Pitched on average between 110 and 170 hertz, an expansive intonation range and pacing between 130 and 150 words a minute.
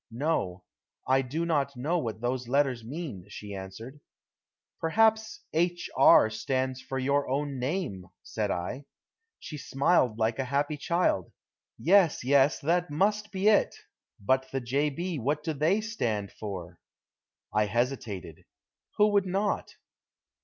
Yes: low, 135 Hz; wide, 6.2 semitones; average, 140 wpm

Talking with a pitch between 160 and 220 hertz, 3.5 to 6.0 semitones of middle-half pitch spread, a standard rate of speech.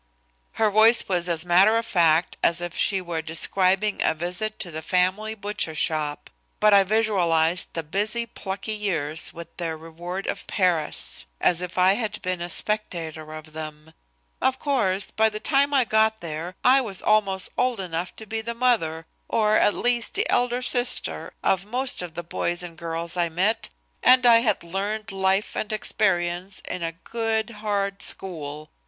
Yes: high, 190 Hz; average, 4.4 semitones; average, 175 wpm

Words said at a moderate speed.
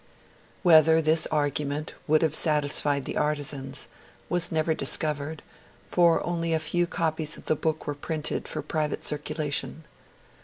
Yes: average, 145 wpm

